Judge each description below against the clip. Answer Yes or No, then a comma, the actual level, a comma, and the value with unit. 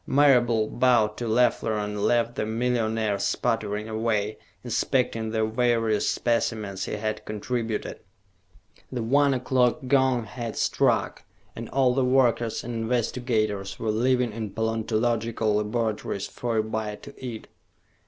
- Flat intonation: Yes, narrow, 2.3 semitones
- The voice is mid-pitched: No, low, 115 Hz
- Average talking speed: No, slow, 130 wpm